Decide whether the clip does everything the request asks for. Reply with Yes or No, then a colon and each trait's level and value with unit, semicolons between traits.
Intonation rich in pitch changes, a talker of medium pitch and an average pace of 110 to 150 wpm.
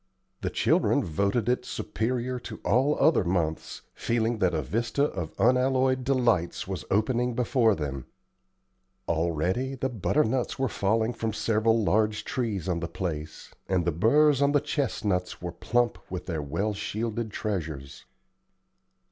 No: wide, 5.9 semitones; low, 110 Hz; average, 140 wpm